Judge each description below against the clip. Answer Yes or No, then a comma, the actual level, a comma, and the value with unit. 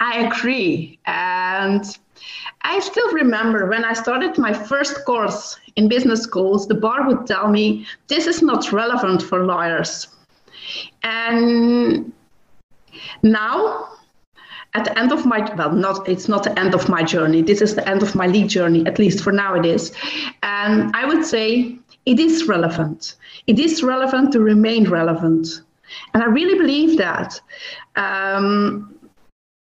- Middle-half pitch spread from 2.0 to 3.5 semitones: No, average, 4.7 semitones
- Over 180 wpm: No, average, 150 wpm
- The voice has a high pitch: Yes, high, 215 Hz